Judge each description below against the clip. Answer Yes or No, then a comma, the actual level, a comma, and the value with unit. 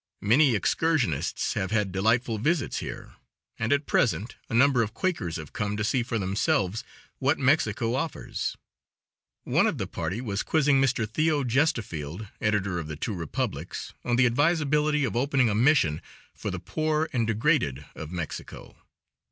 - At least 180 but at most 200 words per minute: No, average, 160 wpm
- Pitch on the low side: Yes, low, 115 Hz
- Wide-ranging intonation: Yes, wide, 6.2 semitones